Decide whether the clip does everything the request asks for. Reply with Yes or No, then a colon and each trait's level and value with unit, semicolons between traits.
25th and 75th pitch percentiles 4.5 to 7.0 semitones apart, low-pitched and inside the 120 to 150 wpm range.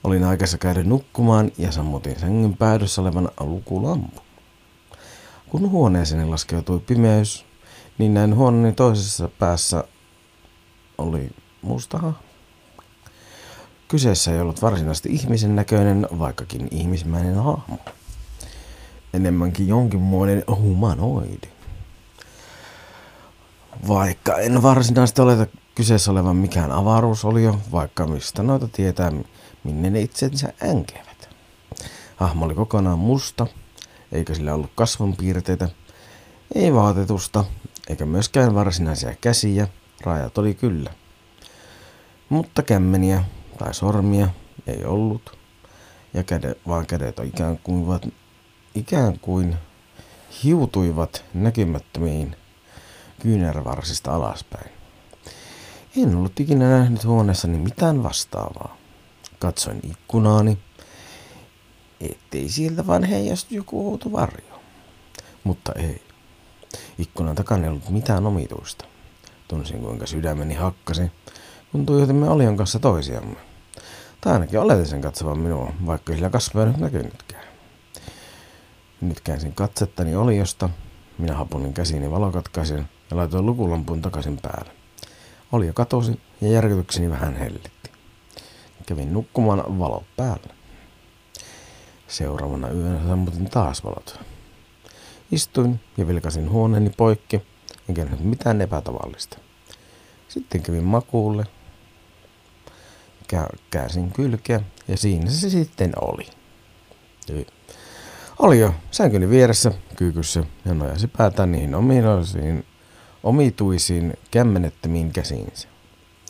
No: average, 4.8 semitones; very low, 95 Hz; average, 100 wpm